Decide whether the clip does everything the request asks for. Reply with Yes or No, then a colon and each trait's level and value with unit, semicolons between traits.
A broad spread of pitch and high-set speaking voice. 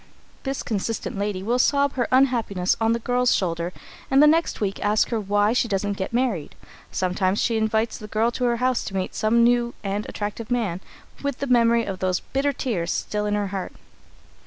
No: average, 3.6 semitones; high, 220 Hz